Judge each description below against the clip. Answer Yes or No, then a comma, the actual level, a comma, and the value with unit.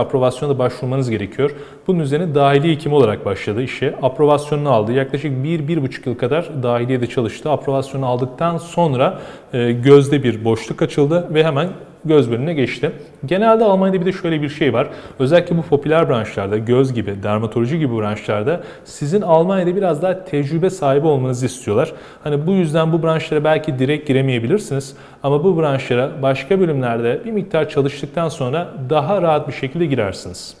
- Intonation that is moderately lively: Yes, average, 4.1 semitones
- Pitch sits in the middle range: Yes, medium, 145 Hz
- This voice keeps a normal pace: No, fast, 155 wpm